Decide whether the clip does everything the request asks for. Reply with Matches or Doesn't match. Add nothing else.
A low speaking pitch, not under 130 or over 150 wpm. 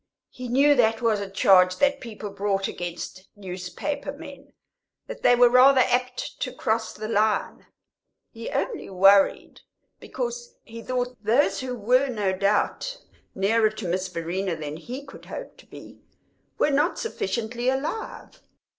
Doesn't match